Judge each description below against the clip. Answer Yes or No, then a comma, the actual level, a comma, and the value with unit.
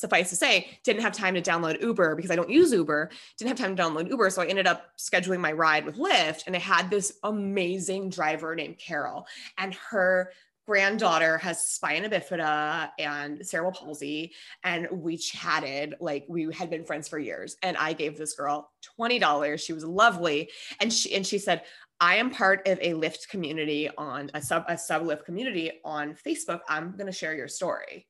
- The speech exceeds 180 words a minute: Yes, average, 200 wpm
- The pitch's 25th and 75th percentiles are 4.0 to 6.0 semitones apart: No, average, 3.4 semitones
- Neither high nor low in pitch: Yes, medium, 170 Hz